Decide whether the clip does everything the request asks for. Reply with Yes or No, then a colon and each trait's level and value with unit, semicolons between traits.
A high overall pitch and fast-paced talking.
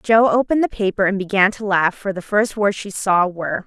Yes: high, 200 Hz; fast, 245 wpm